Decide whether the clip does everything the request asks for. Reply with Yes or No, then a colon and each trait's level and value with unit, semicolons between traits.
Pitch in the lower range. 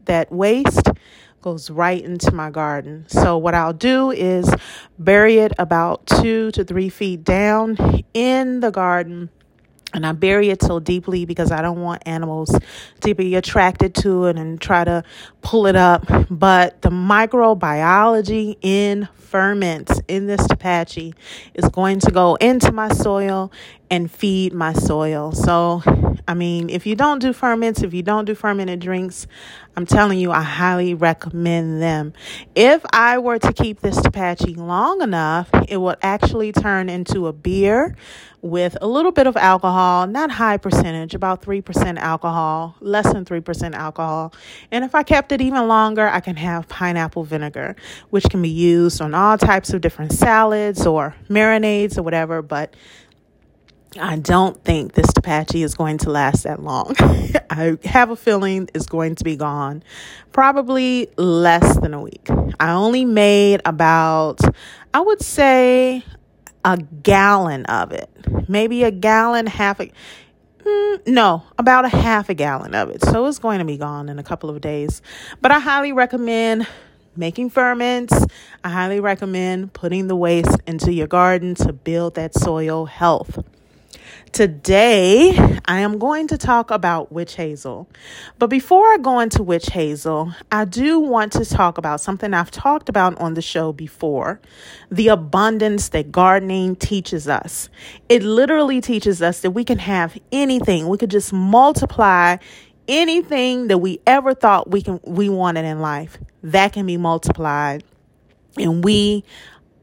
No: medium, 185 Hz